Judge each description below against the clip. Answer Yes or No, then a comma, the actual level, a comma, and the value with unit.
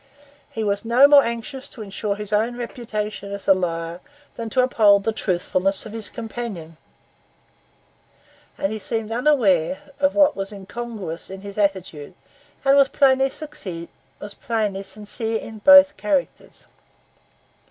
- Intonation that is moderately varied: Yes, average, 3.8 semitones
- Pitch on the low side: No, high, 215 Hz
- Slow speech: Yes, slow, 130 wpm